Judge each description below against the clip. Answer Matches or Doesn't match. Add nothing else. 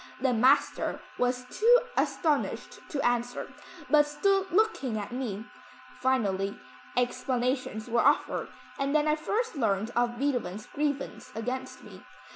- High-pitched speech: Matches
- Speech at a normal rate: Doesn't match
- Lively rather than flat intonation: Doesn't match